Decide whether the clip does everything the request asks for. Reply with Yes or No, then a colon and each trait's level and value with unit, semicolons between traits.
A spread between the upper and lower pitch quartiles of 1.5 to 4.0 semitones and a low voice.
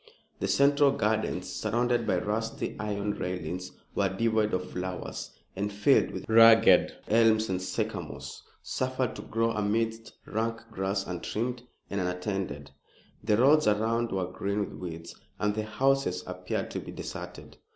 Yes: average, 3.5 semitones; low, 105 Hz